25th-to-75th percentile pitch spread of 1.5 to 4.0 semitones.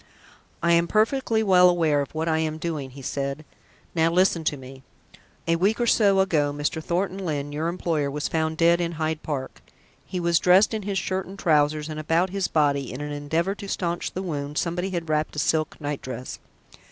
Yes: average, 3.5 semitones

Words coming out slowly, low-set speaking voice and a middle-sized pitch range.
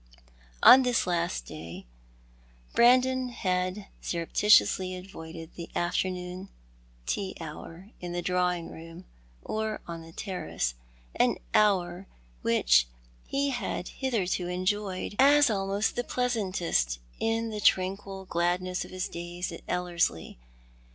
No: slow, 115 wpm; medium, 185 Hz; average, 3.4 semitones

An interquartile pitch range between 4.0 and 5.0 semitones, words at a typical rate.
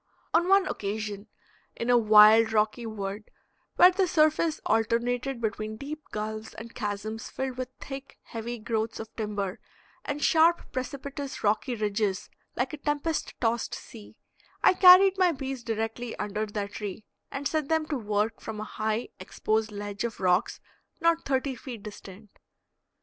Yes: average, 4.6 semitones; average, 150 wpm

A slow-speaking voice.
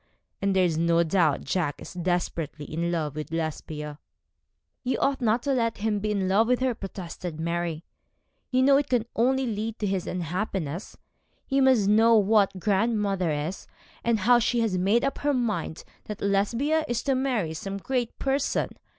No: average, 175 wpm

